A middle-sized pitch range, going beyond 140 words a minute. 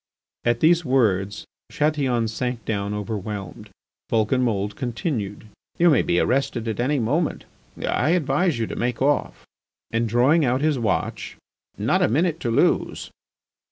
No: average, 5.0 semitones; slow, 135 wpm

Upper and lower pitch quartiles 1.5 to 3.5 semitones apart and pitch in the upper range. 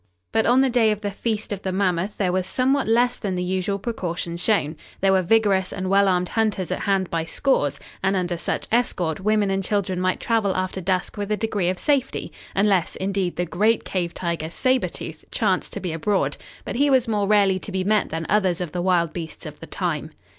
Yes: average, 3.0 semitones; high, 195 Hz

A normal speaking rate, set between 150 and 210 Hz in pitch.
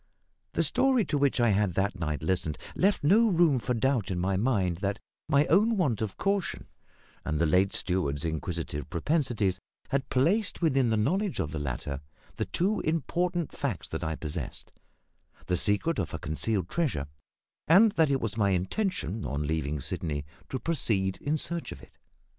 No: average, 175 wpm; low, 110 Hz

